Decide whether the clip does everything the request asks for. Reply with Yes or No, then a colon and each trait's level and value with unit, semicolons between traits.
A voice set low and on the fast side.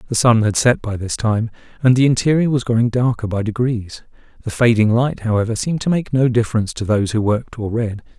Yes: low, 115 Hz; fast, 220 wpm